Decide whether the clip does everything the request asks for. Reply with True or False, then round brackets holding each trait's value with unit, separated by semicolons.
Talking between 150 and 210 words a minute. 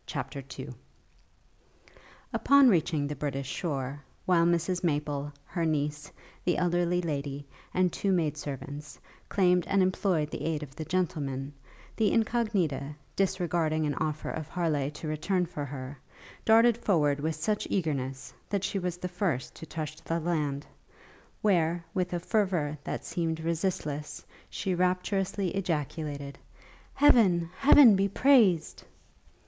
False (135 wpm)